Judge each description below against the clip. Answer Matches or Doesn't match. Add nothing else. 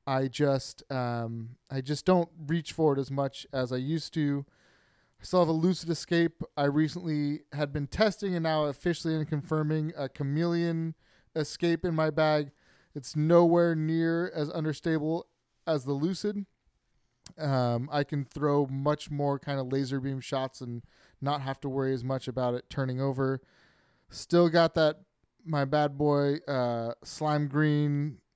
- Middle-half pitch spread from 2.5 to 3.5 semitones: Matches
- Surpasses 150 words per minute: Matches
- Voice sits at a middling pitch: Matches